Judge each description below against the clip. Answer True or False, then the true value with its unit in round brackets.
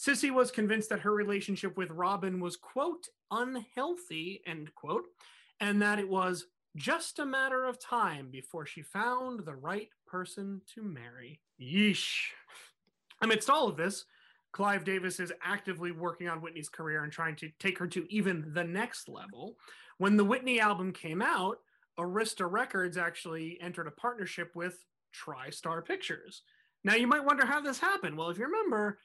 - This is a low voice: False (195 Hz)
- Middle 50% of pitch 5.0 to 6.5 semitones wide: True (5.4 semitones)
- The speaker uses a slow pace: False (165 wpm)